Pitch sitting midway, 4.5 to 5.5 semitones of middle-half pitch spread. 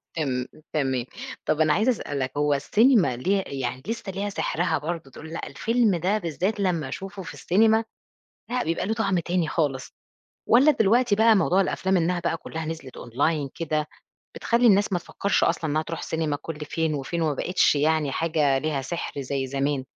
Yes: medium, 165 Hz; average, 5.2 semitones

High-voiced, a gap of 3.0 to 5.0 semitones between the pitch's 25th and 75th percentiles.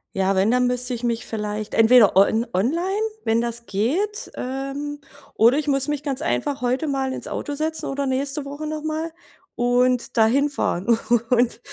Yes: very high, 260 Hz; average, 3.9 semitones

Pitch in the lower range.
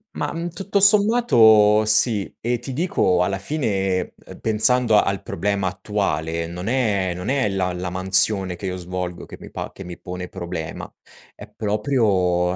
Yes: low, 100 Hz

